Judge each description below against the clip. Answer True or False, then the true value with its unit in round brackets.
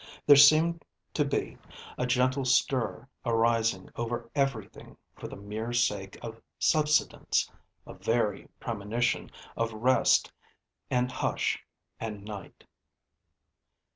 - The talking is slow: True (105 wpm)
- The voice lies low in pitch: True (120 Hz)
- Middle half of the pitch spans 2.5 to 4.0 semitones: True (2.9 semitones)